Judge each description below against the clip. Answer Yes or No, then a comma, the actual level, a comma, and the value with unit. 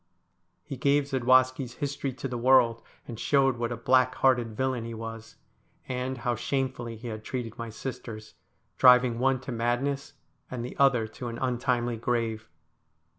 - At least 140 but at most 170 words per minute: Yes, average, 160 wpm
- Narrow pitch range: Yes, narrow, 2.1 semitones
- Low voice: Yes, low, 125 Hz